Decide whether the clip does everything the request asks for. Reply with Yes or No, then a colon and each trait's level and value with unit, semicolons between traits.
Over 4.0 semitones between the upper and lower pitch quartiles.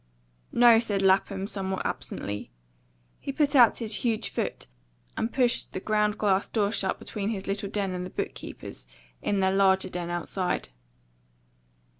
No: narrow, 2.6 semitones